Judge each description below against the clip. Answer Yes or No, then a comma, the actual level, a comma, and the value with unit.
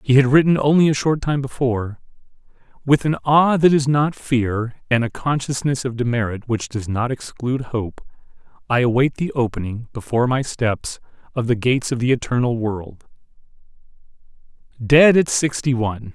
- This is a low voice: Yes, low, 125 Hz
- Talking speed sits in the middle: Yes, average, 160 wpm